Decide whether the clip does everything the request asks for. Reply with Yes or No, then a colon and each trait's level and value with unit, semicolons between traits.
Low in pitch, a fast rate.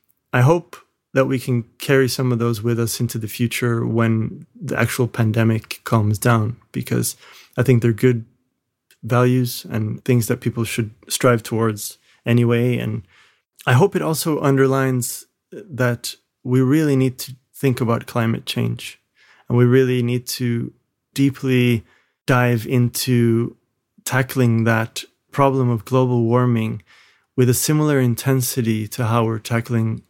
No: low, 120 Hz; average, 140 wpm